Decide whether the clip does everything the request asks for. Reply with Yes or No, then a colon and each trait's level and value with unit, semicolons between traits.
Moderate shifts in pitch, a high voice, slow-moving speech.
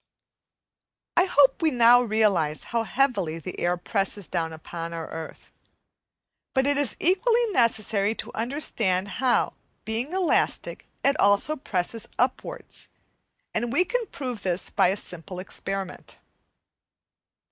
No: wide, 7.0 semitones; high, 220 Hz; slow, 125 wpm